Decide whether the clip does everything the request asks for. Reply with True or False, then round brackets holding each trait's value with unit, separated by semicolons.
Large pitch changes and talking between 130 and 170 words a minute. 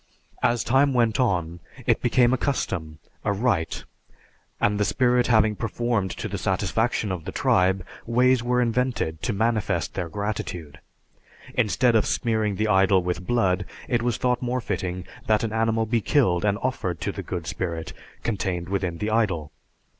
False (4.7 semitones; 165 wpm)